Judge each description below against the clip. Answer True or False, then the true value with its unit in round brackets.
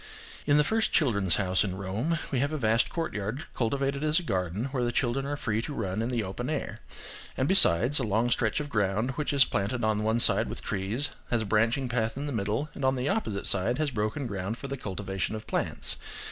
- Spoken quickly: True (225 wpm)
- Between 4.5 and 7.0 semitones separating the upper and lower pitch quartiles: True (4.9 semitones)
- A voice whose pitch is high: False (120 Hz)